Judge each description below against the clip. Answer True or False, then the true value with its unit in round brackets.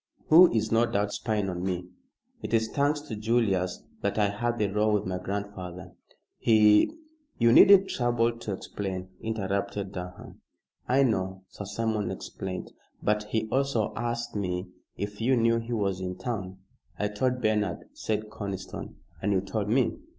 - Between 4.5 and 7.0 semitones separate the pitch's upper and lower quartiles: False (3.2 semitones)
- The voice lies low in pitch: True (105 Hz)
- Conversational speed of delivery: True (165 wpm)